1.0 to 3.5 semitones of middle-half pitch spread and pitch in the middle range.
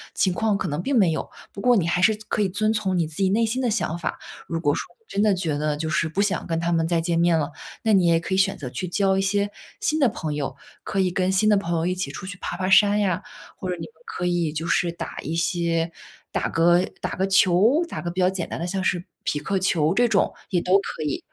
Yes: average, 3.1 semitones; medium, 180 Hz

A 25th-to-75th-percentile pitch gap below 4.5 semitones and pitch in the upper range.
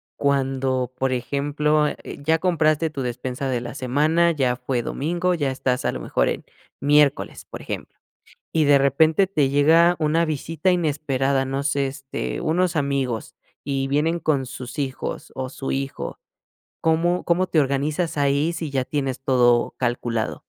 No: average, 3.1 semitones; medium, 140 Hz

